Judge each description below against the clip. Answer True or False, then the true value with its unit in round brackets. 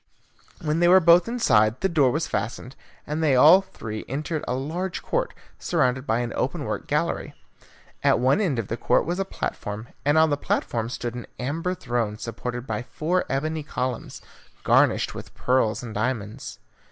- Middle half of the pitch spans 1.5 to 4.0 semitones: False (5.2 semitones)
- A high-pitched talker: False (135 Hz)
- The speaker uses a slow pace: False (175 wpm)